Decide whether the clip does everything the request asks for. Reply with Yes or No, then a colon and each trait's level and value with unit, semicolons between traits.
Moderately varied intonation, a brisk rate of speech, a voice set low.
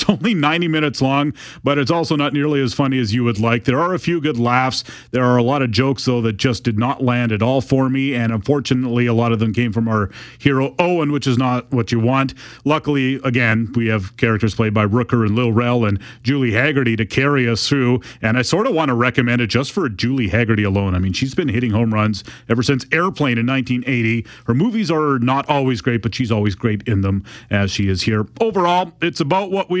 Yes: average, 3.4 semitones; fast, 240 wpm; low, 125 Hz